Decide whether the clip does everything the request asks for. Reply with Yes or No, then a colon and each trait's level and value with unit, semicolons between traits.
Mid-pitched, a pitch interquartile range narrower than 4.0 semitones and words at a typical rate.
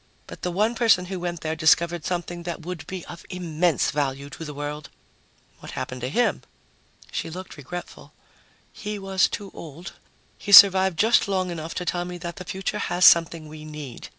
Yes: medium, 175 Hz; average, 3.1 semitones; average, 185 wpm